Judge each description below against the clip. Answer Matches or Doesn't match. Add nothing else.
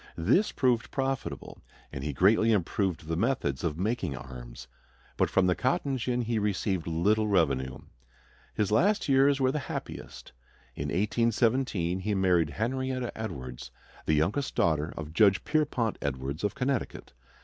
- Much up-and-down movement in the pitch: Matches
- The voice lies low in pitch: Matches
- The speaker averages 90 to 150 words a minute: Matches